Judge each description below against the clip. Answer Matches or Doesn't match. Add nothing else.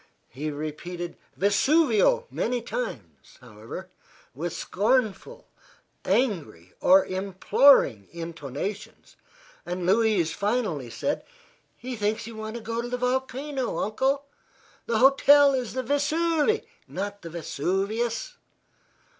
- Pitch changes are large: Matches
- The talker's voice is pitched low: Doesn't match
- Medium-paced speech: Doesn't match